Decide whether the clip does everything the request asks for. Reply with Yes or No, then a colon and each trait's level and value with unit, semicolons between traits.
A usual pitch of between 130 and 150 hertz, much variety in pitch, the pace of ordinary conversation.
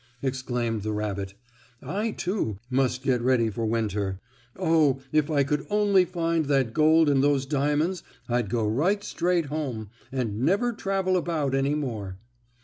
Yes: medium, 140 Hz; wide, 6.2 semitones; average, 150 wpm